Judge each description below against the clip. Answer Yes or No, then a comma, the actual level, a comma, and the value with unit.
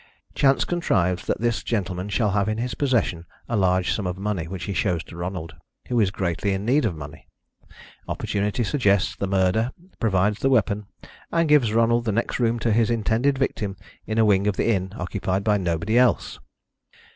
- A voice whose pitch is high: No, low, 105 Hz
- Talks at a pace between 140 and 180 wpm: No, average, 190 wpm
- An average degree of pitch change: Yes, average, 3.9 semitones